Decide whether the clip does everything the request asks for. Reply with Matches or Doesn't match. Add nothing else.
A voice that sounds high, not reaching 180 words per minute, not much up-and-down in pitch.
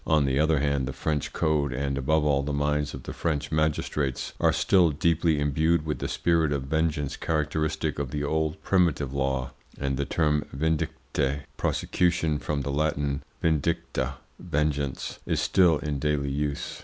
Doesn't match